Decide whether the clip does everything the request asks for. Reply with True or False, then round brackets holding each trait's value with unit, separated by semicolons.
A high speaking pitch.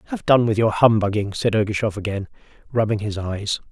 False (105 Hz)